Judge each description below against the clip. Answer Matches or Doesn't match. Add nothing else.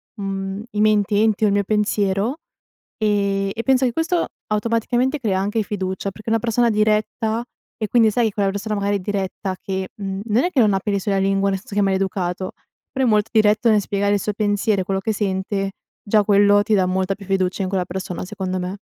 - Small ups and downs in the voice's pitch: Matches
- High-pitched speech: Matches